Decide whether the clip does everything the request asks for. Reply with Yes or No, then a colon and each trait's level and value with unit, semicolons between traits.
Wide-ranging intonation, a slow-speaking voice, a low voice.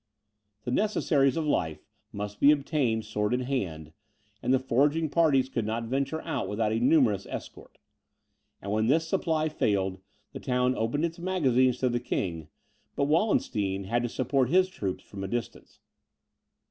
No: wide, 6.0 semitones; average, 160 wpm; low, 125 Hz